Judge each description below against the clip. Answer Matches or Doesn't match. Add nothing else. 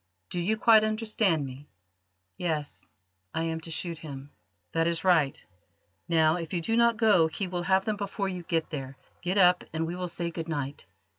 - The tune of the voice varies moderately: Matches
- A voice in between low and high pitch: Matches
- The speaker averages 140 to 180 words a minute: Doesn't match